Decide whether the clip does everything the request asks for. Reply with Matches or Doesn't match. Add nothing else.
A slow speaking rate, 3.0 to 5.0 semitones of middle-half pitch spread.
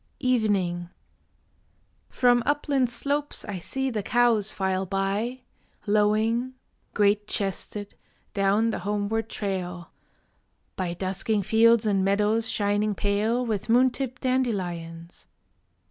Matches